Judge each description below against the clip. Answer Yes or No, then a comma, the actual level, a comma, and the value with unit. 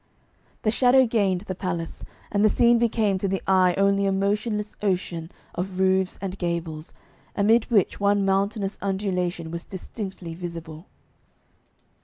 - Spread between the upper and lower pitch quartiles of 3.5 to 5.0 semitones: No, narrow, 2.5 semitones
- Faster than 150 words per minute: No, average, 140 wpm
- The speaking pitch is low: No, high, 195 Hz